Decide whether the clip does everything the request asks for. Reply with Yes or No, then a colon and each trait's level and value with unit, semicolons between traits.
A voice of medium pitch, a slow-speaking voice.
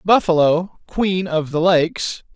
Yes: medium, 175 Hz; slow, 130 wpm